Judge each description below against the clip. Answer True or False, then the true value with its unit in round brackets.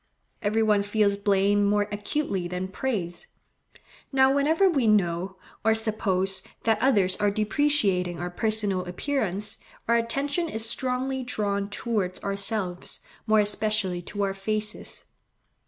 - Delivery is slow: True (125 wpm)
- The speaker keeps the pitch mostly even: False (3.0 semitones)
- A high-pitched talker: True (210 Hz)